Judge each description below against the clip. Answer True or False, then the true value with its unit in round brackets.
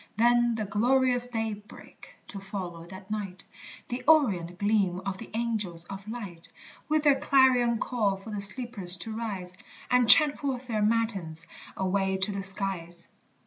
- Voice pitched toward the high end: True (210 Hz)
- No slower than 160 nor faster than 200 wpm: False (150 wpm)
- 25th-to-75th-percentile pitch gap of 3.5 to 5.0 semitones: True (4.0 semitones)